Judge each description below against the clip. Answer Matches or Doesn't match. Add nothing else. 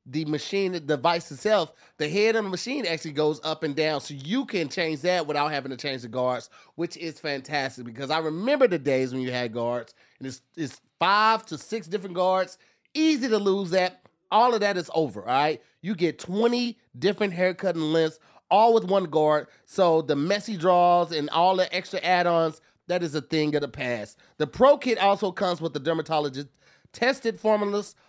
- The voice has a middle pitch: Matches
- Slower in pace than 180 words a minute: Doesn't match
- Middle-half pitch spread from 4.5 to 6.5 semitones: Matches